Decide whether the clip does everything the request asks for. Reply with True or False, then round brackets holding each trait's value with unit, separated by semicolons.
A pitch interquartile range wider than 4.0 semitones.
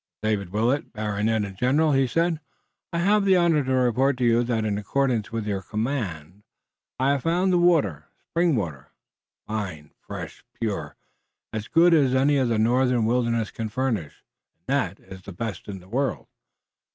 True (5.1 semitones)